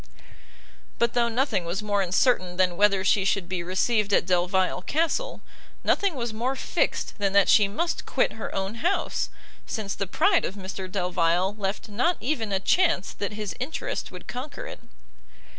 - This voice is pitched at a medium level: No, high, 205 Hz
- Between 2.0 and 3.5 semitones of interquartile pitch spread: No, average, 4.8 semitones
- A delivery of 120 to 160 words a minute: No, average, 170 wpm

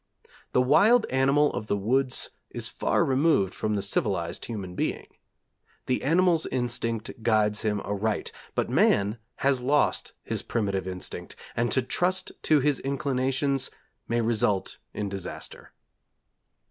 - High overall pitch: No, low, 120 Hz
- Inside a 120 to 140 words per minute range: Yes, slow, 135 wpm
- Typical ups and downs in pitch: Yes, average, 4.9 semitones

